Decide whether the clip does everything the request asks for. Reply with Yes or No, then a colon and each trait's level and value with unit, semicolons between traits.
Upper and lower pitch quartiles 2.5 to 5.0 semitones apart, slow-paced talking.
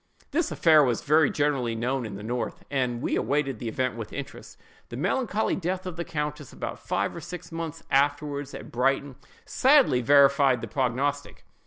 No: average, 3.6 semitones; average, 175 wpm